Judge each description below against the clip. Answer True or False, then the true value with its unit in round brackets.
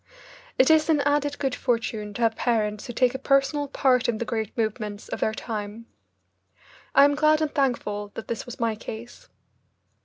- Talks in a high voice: True (240 Hz)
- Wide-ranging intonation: False (4.2 semitones)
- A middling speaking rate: True (185 wpm)